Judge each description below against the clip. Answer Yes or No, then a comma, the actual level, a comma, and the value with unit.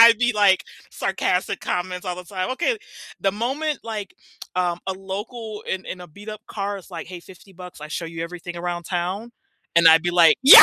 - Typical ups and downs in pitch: Yes, average, 3.3 semitones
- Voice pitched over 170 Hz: Yes, medium, 185 Hz